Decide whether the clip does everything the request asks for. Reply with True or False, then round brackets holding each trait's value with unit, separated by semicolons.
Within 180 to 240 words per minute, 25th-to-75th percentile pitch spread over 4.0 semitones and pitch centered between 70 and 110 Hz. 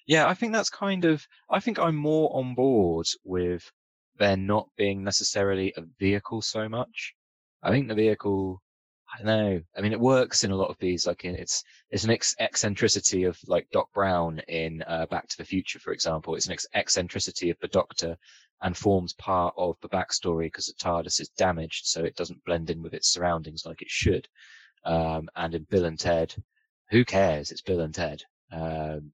True (200 wpm; 4.6 semitones; 95 Hz)